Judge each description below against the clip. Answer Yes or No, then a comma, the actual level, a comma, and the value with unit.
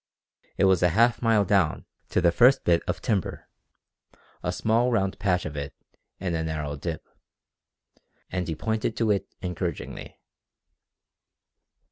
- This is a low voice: Yes, very low, 95 Hz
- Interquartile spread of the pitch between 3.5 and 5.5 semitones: Yes, average, 5.0 semitones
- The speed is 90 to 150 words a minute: Yes, average, 140 wpm